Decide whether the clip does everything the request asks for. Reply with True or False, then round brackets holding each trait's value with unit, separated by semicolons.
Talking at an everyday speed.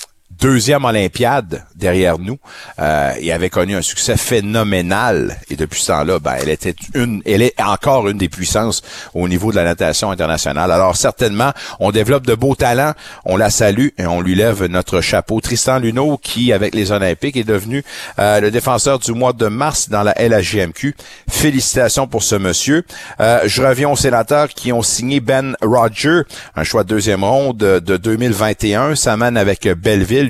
True (180 wpm)